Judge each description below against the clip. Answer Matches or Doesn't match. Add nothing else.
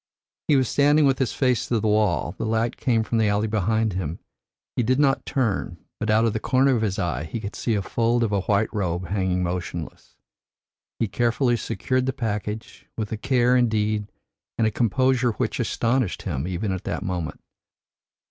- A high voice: Doesn't match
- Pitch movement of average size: Matches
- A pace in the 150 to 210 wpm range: Matches